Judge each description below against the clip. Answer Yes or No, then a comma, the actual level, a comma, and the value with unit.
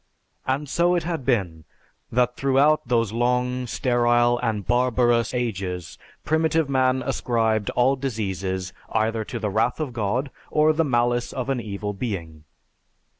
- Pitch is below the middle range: Yes, low, 120 Hz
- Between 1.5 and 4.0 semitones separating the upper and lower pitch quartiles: Yes, average, 3.3 semitones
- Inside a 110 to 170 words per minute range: Yes, average, 140 wpm